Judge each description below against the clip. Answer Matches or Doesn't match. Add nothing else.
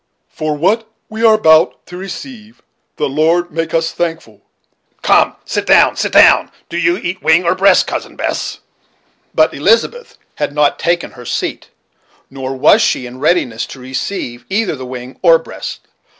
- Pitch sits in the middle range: Matches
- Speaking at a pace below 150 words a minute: Doesn't match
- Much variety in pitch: Matches